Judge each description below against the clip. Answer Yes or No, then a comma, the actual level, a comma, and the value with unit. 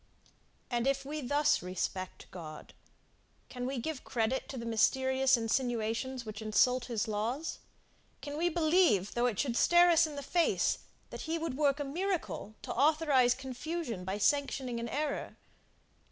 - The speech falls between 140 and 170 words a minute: Yes, average, 155 wpm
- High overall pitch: Yes, very high, 260 Hz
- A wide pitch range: No, average, 4.6 semitones